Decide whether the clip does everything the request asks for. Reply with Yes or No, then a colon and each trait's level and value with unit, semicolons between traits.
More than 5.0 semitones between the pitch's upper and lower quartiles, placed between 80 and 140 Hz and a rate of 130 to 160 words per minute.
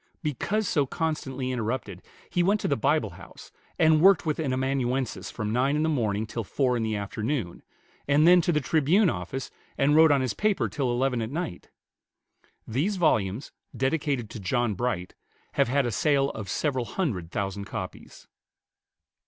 No: wide, 5.5 semitones; low, 135 Hz; average, 170 wpm